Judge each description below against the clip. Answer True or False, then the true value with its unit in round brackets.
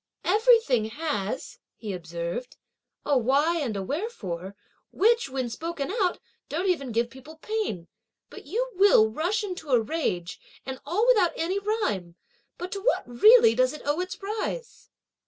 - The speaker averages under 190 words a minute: True (155 wpm)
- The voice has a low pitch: False (305 Hz)